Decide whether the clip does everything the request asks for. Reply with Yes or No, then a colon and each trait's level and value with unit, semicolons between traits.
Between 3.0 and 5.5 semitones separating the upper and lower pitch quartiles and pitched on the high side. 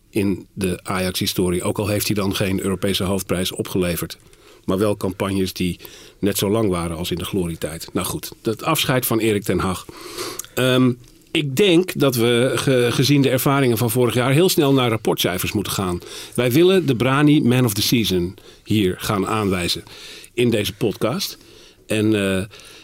No: average, 5.0 semitones; low, 110 Hz